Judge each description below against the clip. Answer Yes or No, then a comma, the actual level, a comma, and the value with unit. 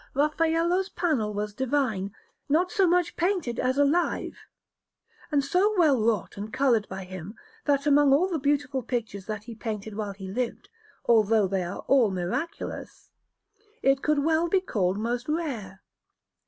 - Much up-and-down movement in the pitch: Yes, wide, 6.6 semitones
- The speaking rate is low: No, average, 155 wpm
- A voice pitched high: Yes, very high, 260 Hz